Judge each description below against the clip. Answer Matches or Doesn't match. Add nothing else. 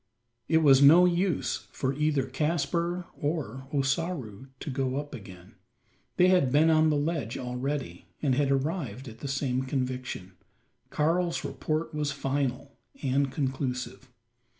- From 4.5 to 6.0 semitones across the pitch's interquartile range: Doesn't match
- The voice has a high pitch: Doesn't match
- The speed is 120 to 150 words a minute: Matches